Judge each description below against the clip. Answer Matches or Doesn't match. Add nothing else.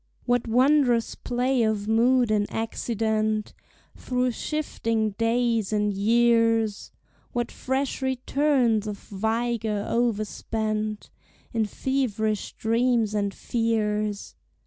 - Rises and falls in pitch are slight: Matches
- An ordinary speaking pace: Doesn't match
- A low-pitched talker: Doesn't match